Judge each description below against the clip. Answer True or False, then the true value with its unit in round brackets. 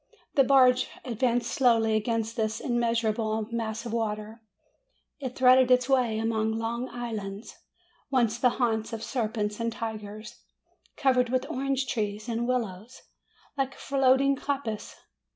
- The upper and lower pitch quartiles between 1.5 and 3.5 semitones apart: True (2.5 semitones)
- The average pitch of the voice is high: True (235 Hz)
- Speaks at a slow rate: True (130 wpm)